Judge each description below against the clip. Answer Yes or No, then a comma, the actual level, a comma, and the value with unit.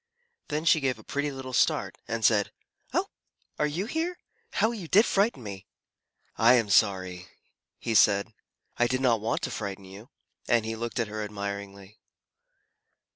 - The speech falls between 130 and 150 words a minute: No, average, 165 wpm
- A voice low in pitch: Yes, low, 115 Hz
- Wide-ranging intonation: Yes, wide, 5.8 semitones